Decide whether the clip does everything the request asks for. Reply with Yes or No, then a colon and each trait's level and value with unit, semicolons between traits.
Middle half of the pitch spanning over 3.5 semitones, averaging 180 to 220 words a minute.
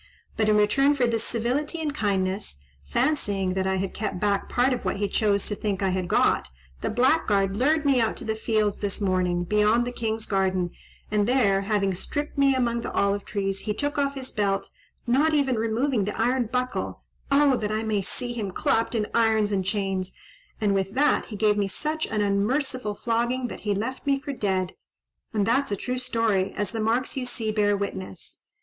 Yes: average, 4.1 semitones; average, 200 wpm